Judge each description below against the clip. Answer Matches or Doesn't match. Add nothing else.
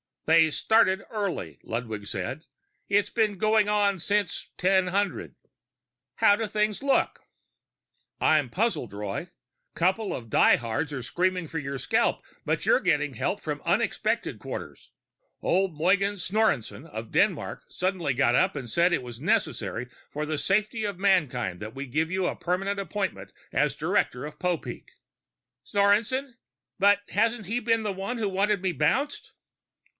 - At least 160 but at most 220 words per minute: Doesn't match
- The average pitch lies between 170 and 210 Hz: Matches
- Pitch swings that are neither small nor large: Doesn't match